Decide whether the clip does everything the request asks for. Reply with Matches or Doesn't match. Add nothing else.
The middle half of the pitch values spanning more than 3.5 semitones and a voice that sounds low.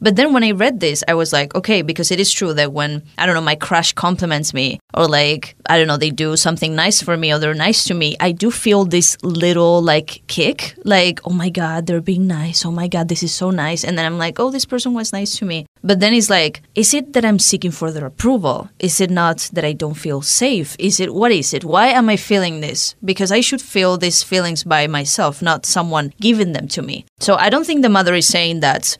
Doesn't match